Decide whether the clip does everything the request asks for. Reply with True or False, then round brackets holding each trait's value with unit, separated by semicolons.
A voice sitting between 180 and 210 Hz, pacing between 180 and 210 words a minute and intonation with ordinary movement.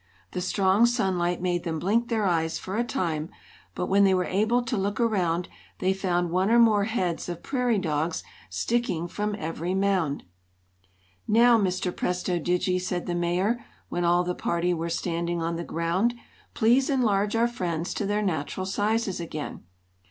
False (185 Hz; 170 wpm; 3.5 semitones)